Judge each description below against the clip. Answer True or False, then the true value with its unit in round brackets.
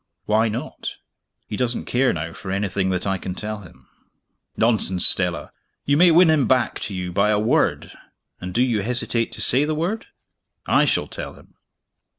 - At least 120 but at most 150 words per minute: False (180 wpm)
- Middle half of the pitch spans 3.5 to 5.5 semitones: True (5.2 semitones)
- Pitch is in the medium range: False (110 Hz)